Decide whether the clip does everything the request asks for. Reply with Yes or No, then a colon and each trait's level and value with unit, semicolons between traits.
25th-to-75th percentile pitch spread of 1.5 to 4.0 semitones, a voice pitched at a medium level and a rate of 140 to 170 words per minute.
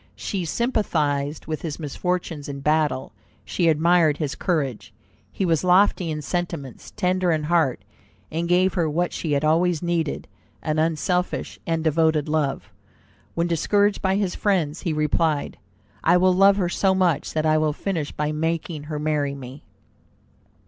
Yes: average, 2.9 semitones; medium, 160 Hz; average, 155 wpm